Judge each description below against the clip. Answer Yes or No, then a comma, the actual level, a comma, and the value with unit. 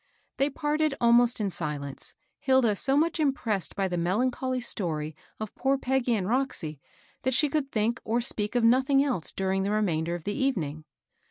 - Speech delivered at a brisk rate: No, average, 180 wpm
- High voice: Yes, high, 235 Hz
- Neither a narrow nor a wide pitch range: No, wide, 6.1 semitones